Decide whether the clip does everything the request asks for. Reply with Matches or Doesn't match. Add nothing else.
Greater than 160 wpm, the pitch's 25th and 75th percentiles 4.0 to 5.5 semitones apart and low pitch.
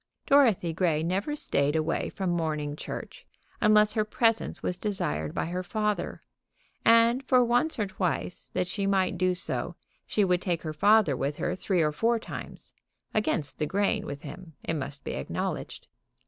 Doesn't match